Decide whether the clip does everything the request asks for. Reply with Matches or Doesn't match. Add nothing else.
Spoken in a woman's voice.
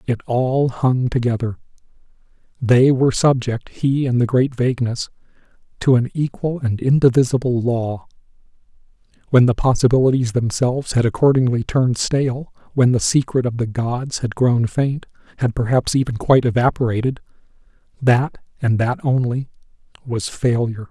Doesn't match